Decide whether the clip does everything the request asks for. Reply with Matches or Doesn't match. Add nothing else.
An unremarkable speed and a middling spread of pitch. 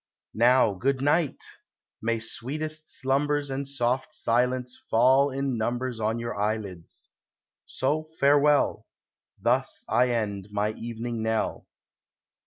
Doesn't match